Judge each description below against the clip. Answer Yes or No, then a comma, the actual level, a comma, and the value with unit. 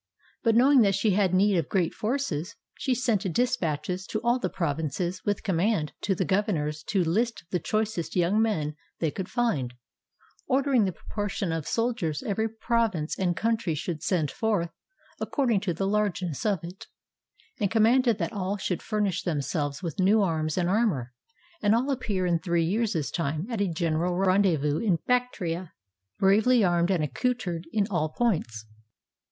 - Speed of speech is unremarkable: Yes, average, 165 wpm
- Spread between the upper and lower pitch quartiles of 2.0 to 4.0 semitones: No, average, 4.9 semitones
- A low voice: No, high, 190 Hz